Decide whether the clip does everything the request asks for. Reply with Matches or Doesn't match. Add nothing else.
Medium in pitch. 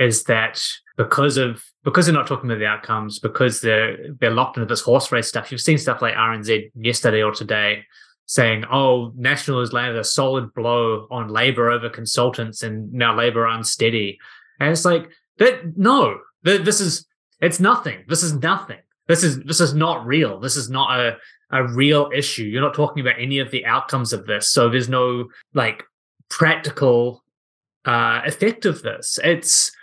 Doesn't match